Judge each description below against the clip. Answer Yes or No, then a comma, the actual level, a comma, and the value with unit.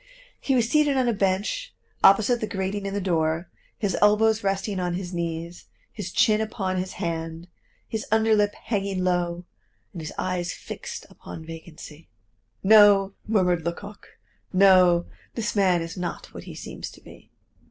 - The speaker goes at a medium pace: Yes, average, 160 wpm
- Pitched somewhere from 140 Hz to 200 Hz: Yes, high, 190 Hz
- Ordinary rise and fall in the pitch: Yes, average, 3.3 semitones